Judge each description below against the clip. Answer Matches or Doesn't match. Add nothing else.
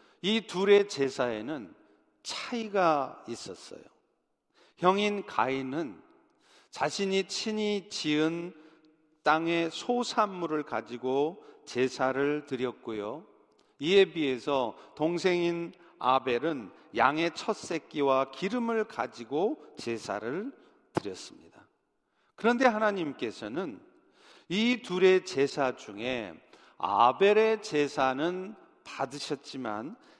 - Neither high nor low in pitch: Matches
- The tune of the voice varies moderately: Doesn't match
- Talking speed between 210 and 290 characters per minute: Doesn't match